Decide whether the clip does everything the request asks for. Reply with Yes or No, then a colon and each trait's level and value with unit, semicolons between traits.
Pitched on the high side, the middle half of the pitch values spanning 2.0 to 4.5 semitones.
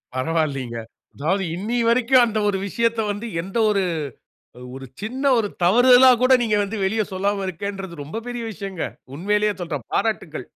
No: high, 200 Hz; average, 4.9 semitones